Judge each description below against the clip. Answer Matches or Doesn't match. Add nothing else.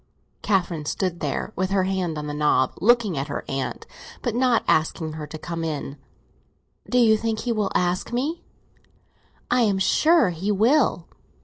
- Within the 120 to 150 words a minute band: Doesn't match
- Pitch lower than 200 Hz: Matches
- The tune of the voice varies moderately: Doesn't match